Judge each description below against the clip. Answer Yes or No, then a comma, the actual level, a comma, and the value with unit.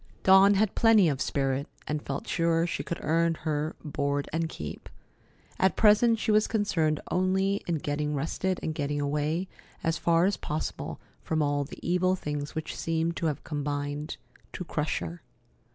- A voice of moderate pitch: Yes, medium, 160 Hz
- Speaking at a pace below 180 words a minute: Yes, average, 170 wpm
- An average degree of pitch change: Yes, average, 3.9 semitones